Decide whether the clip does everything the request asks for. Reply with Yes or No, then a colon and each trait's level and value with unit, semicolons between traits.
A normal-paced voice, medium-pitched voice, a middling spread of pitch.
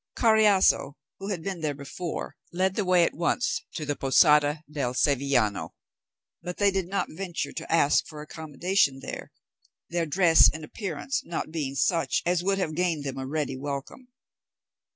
Yes: average, 165 wpm; medium, 165 Hz; average, 4.4 semitones